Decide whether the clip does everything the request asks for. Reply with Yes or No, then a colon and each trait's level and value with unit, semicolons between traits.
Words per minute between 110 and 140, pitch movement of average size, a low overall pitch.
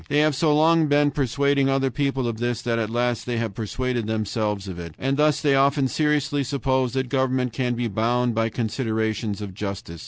No: fast, 205 wpm; average, 3.8 semitones; low, 125 Hz